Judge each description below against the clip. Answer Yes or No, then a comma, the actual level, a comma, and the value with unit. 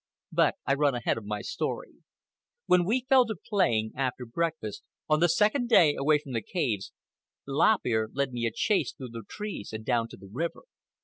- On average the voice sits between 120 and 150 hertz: Yes, medium, 140 Hz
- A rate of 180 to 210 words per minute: Yes, average, 195 wpm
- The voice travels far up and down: Yes, wide, 7.6 semitones